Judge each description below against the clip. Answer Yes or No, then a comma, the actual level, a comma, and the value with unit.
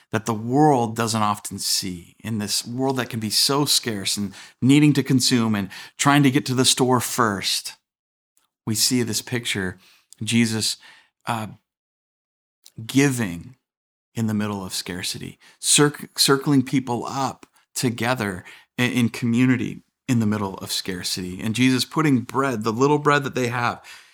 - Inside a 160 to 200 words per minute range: No, average, 150 wpm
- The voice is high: No, low, 120 Hz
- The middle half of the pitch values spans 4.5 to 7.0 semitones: No, average, 3.8 semitones